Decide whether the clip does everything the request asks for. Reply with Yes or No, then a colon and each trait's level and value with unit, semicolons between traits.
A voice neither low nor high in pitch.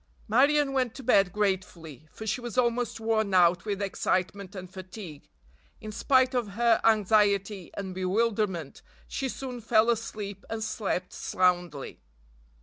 No: high, 210 Hz